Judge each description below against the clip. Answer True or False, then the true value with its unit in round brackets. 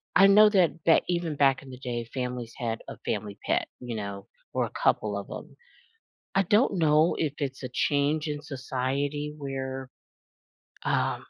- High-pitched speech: False (140 Hz)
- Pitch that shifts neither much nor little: True (3.9 semitones)